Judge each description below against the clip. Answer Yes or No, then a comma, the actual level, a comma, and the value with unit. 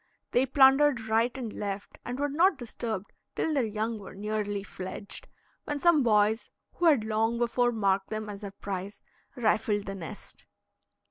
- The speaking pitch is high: Yes, high, 220 Hz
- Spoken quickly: No, average, 160 wpm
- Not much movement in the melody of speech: No, average, 3.6 semitones